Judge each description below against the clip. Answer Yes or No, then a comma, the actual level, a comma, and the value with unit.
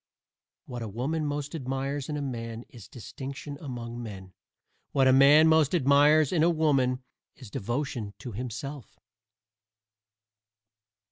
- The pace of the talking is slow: Yes, slow, 130 wpm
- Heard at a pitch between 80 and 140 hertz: Yes, low, 135 Hz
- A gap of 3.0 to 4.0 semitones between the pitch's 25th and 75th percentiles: Yes, average, 3.5 semitones